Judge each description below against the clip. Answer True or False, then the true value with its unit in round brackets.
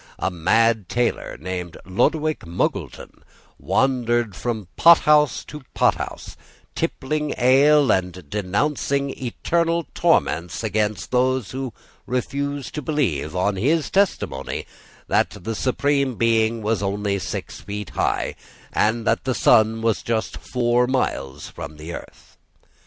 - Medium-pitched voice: False (115 Hz)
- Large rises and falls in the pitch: True (5.7 semitones)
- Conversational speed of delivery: False (120 wpm)